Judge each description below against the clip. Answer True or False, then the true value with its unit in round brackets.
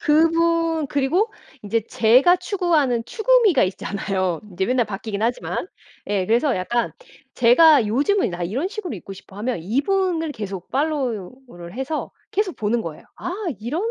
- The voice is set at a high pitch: True (255 Hz)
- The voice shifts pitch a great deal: True (8.1 semitones)